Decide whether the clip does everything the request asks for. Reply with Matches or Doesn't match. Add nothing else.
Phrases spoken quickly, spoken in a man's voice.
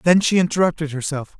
Doesn't match